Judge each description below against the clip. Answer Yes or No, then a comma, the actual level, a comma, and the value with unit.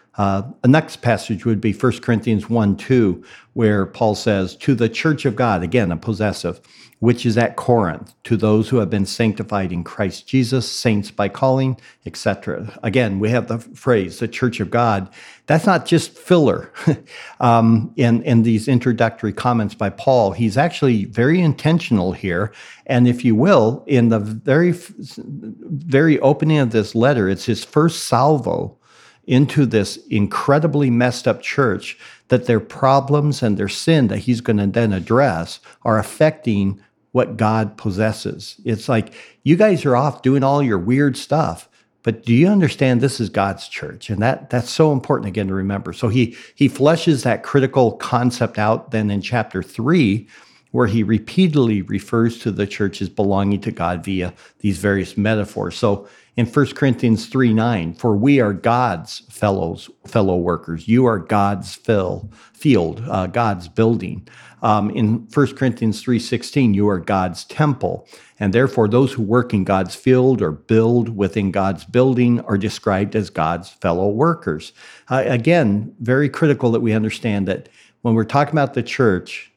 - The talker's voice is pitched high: No, low, 115 Hz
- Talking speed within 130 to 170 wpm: Yes, average, 165 wpm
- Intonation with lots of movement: No, average, 4.2 semitones